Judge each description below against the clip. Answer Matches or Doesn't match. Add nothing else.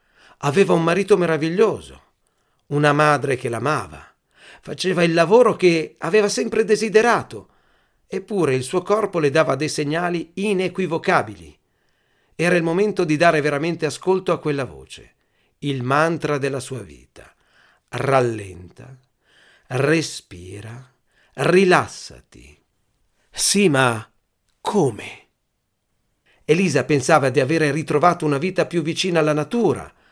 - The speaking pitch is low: Doesn't match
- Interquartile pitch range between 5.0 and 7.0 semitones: Matches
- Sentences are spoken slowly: Matches